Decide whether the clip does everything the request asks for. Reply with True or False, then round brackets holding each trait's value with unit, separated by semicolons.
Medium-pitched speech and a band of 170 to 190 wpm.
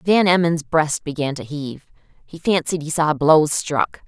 True (155 Hz; 175 wpm)